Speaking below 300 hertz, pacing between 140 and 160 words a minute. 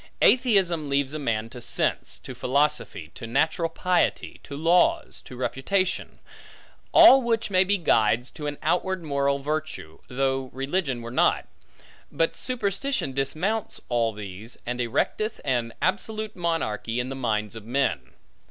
Yes: medium, 140 Hz; average, 145 wpm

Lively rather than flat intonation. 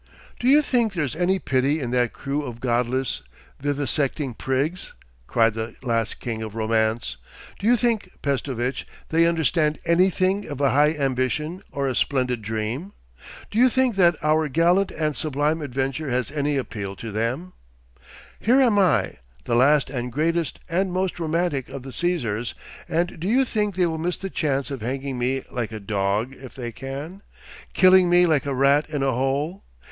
Yes: wide, 5.7 semitones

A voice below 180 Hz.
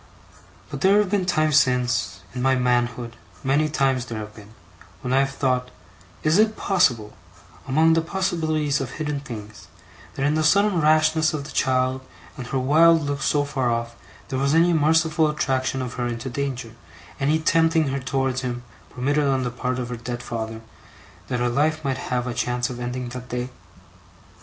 Yes: low, 135 Hz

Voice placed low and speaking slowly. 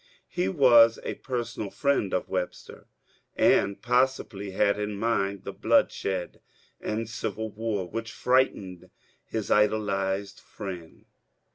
Yes: low, 105 Hz; slow, 125 wpm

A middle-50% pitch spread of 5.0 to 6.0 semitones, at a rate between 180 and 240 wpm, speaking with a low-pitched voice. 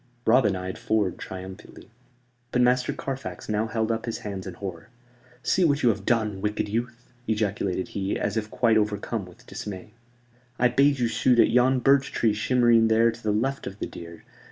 No: average, 3.3 semitones; average, 185 wpm; low, 110 Hz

